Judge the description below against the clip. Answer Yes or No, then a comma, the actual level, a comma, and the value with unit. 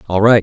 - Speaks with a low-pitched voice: Yes, low, 105 Hz